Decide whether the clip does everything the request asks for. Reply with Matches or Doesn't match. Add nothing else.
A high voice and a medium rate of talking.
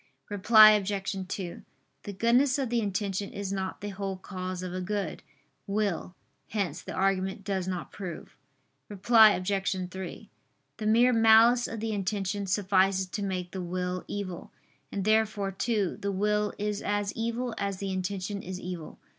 Matches